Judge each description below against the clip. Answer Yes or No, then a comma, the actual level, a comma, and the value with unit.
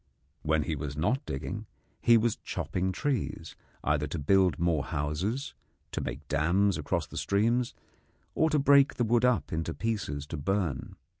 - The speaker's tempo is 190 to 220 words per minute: No, average, 160 wpm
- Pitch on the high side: No, very low, 95 Hz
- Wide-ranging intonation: Yes, wide, 7.5 semitones